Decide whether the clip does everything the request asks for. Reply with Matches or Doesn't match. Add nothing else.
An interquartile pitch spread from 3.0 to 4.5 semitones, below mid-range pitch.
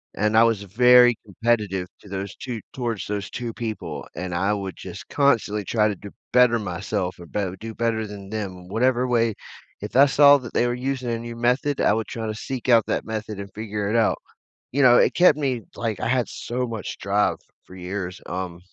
Matches